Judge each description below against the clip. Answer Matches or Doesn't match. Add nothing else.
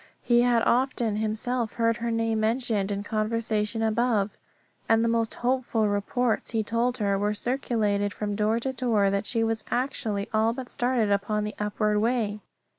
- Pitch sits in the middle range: Doesn't match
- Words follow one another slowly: Doesn't match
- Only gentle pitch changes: Matches